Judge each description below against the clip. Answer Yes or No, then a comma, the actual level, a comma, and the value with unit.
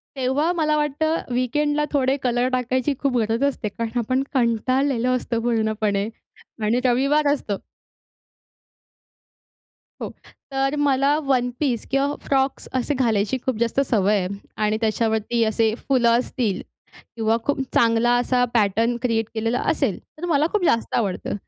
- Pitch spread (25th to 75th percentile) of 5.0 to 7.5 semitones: No, average, 3.3 semitones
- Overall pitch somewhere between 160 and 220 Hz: No, high, 245 Hz